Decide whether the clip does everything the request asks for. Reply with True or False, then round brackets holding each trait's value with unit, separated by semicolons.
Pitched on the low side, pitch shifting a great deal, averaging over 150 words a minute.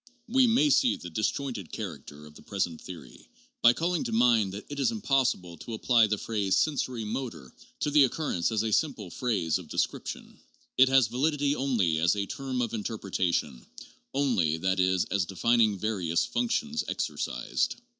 True (110 Hz; 6.7 semitones; 175 wpm)